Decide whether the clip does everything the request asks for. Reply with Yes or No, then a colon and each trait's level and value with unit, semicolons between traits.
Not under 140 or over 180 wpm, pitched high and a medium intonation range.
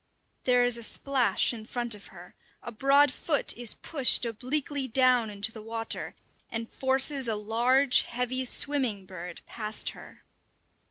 Yes: average, 150 wpm; high, 245 Hz; average, 3.0 semitones